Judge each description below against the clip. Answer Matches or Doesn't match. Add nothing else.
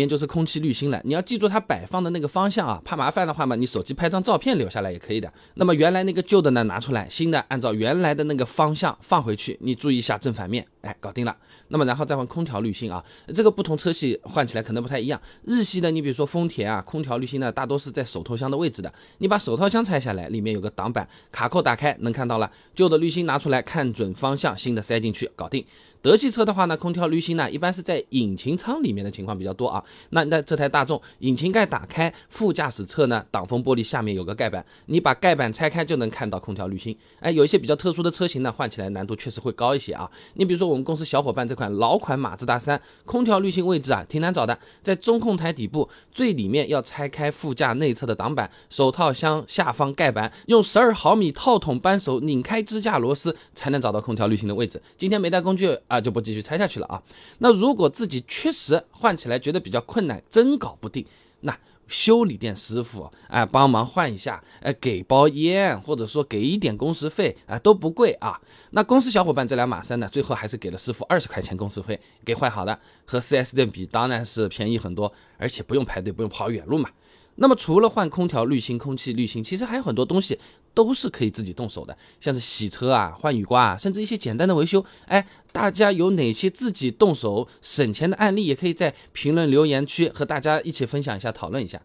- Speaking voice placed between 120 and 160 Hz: Matches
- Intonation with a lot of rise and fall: Matches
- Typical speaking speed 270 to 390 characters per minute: Matches